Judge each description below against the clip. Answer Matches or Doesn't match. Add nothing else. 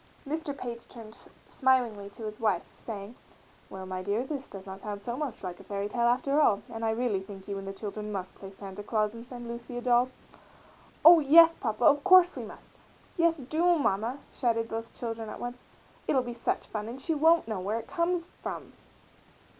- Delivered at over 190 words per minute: Matches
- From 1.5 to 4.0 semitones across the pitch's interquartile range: Doesn't match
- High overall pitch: Matches